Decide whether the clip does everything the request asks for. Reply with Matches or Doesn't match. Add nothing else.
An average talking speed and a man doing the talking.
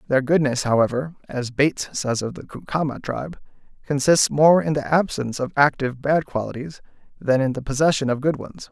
Matches